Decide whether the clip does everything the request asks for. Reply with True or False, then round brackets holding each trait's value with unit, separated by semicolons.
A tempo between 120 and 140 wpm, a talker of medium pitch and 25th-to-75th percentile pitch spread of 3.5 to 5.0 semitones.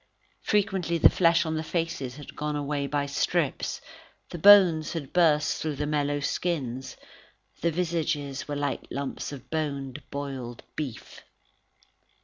False (135 wpm; 150 Hz; 2.9 semitones)